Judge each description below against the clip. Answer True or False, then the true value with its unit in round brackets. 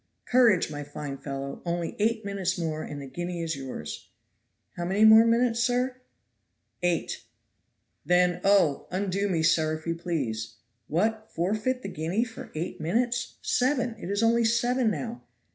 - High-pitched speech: False (180 Hz)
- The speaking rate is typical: True (155 wpm)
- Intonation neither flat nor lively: False (6.2 semitones)